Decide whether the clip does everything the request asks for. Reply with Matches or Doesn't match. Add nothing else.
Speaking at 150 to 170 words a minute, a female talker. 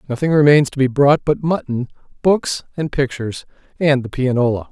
Doesn't match